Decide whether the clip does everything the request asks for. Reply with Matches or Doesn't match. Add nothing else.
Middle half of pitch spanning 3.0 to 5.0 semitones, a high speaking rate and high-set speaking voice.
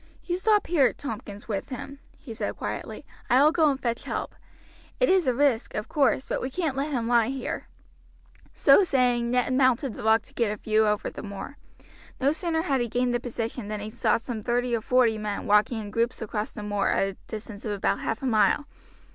Matches